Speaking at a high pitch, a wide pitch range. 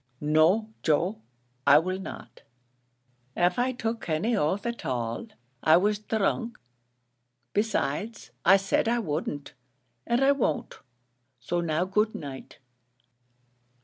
Yes: high, 195 Hz; wide, 6.2 semitones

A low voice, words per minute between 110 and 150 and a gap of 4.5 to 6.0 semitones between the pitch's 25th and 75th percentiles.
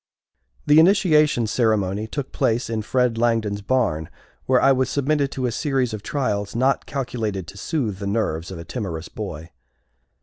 No: low, 115 Hz; average, 165 wpm; average, 4.8 semitones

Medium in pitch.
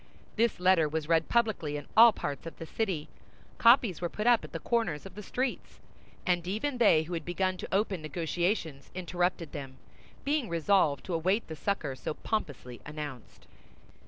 Yes: medium, 175 Hz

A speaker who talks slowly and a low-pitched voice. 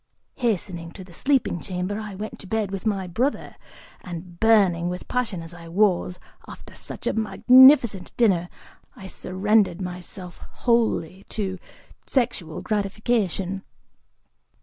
No: slow, 125 wpm; high, 195 Hz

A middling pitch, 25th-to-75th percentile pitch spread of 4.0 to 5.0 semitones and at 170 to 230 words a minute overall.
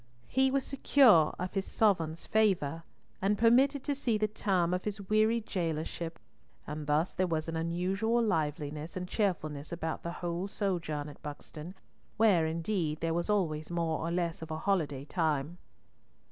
No: medium, 175 Hz; average, 4.7 semitones; average, 160 wpm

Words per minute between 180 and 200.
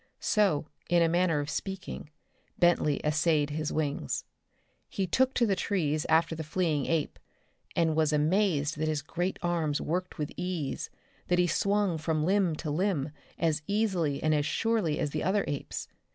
No: average, 165 wpm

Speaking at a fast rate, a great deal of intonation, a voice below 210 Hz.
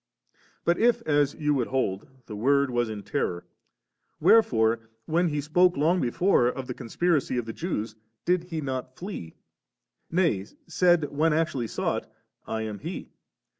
No: average, 160 wpm; wide, 6.7 semitones; medium, 140 Hz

